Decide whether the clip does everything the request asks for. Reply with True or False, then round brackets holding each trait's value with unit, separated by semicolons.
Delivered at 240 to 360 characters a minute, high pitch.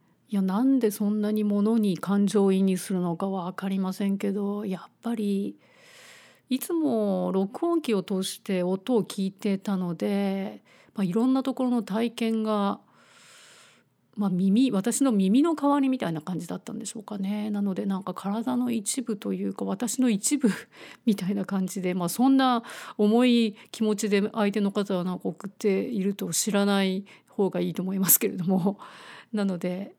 True (320 characters per minute; 205 Hz)